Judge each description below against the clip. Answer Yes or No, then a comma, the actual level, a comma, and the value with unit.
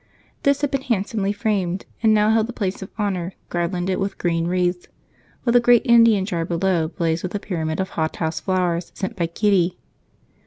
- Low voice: No, high, 190 Hz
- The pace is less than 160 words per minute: No, average, 185 wpm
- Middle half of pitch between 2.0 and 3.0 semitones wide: No, average, 3.7 semitones